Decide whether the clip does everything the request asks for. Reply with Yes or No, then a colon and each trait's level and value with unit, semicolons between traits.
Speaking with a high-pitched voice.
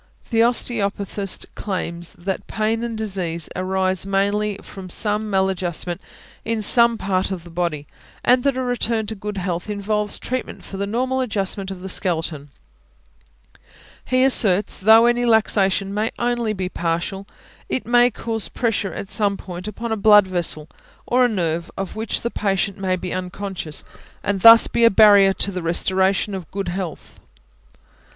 Yes: high, 200 Hz